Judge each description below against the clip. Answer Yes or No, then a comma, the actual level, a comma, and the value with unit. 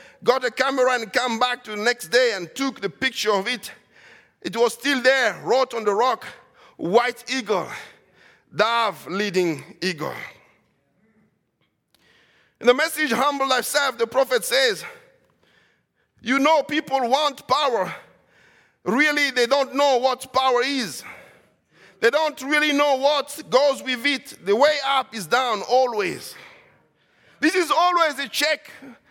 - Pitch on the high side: Yes, very high, 260 Hz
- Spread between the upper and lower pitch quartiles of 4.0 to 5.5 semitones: No, average, 3.4 semitones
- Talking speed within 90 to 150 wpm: Yes, average, 140 wpm